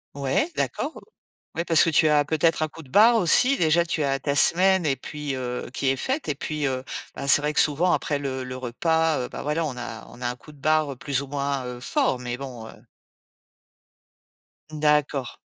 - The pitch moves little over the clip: No, average, 3.3 semitones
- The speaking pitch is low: No, medium, 145 Hz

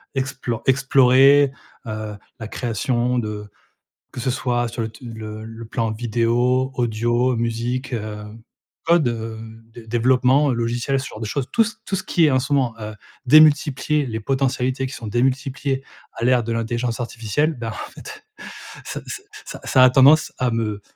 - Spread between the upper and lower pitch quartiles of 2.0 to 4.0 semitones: Yes, average, 2.8 semitones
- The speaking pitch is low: Yes, low, 125 Hz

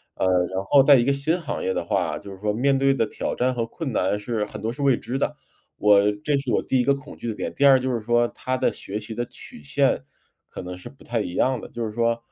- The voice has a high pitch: No, low, 120 Hz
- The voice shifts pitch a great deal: No, average, 4.4 semitones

